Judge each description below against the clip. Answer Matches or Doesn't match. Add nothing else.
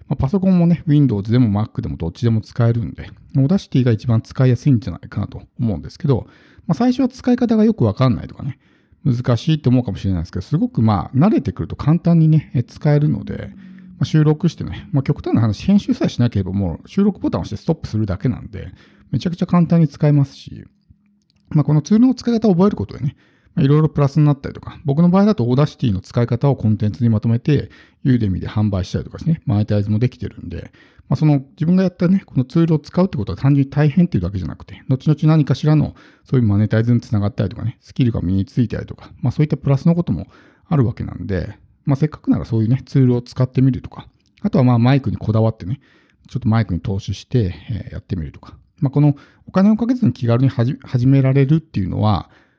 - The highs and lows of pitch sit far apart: Matches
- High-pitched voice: Doesn't match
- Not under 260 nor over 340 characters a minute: Doesn't match